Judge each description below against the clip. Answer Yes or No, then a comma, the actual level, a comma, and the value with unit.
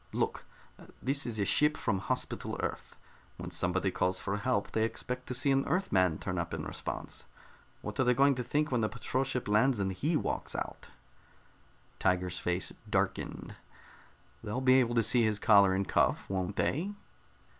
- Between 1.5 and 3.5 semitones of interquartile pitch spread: No, average, 5.3 semitones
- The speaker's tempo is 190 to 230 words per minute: No, average, 175 wpm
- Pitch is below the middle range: Yes, low, 115 Hz